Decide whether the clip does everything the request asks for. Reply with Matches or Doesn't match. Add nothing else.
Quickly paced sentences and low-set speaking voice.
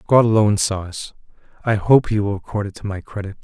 Matches